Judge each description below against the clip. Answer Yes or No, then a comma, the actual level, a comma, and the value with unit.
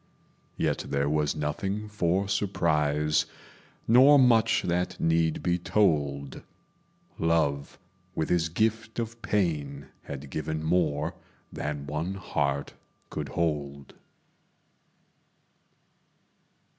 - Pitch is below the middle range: Yes, very low, 80 Hz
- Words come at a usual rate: No, slow, 95 wpm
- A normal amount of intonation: Yes, average, 4.9 semitones